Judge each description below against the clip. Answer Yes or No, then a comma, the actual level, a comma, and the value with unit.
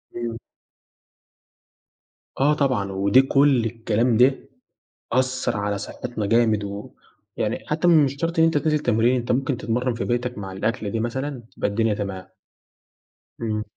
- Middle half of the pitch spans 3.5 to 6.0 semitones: Yes, average, 3.8 semitones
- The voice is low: Yes, low, 120 Hz